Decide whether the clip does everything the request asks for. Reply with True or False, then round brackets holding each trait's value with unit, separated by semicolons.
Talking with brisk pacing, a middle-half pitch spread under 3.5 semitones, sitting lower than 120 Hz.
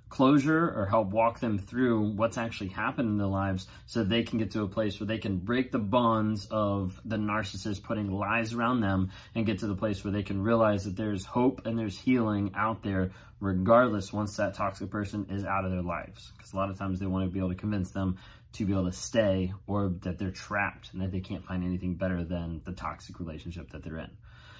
True (230 wpm; 2.9 semitones; 100 Hz)